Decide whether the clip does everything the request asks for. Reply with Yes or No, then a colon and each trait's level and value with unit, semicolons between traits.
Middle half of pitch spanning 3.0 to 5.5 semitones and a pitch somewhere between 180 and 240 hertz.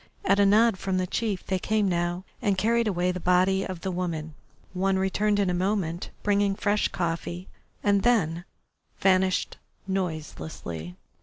No: narrow, 2.4 semitones; high, 190 Hz